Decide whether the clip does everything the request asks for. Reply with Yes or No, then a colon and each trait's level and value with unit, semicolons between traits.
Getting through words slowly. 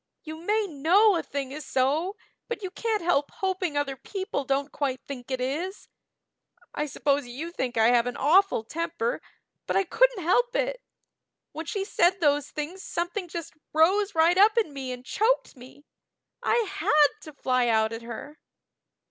No: average, 175 wpm